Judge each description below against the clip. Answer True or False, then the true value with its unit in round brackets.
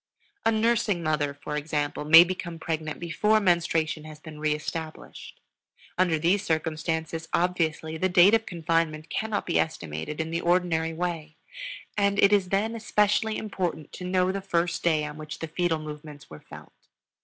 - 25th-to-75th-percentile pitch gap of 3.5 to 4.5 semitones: False (3.0 semitones)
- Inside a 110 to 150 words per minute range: False (160 wpm)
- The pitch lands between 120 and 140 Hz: False (165 Hz)